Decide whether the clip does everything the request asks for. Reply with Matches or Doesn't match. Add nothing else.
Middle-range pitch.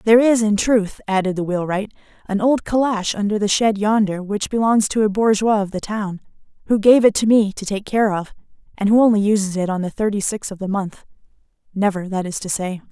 Doesn't match